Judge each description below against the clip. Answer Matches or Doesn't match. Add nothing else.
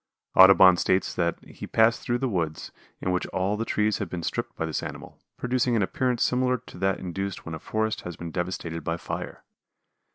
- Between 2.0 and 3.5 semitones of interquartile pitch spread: Doesn't match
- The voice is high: Doesn't match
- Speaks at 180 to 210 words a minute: Matches